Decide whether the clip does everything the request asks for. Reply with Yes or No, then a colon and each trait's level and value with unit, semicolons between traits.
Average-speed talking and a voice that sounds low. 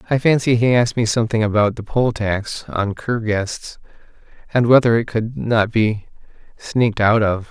Yes: average, 175 wpm; low, 115 Hz